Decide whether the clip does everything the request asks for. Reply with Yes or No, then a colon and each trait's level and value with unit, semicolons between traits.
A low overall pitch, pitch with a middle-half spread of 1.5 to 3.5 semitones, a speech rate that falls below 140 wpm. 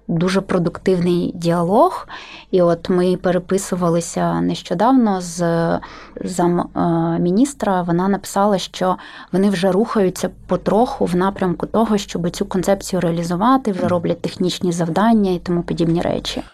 No: medium, 185 Hz; narrow, 2.4 semitones; average, 120 wpm